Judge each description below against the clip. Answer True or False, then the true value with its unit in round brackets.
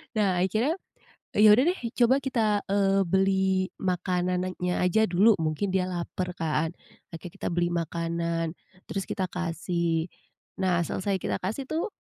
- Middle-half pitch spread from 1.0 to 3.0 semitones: True (2.7 semitones)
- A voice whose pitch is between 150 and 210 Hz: True (185 Hz)